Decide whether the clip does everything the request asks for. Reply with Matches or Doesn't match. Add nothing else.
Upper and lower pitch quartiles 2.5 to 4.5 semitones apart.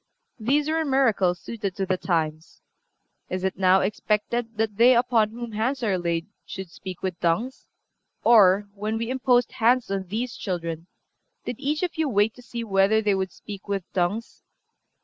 Matches